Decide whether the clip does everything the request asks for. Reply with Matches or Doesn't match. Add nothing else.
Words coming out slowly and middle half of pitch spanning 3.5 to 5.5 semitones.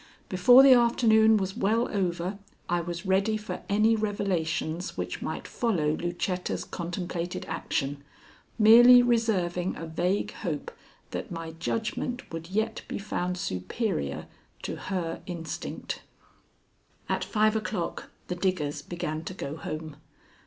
Matches